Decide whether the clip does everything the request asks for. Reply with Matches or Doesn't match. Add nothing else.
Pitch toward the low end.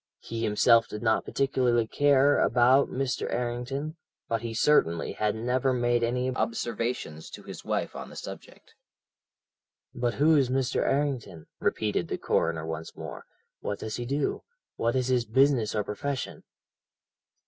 Matches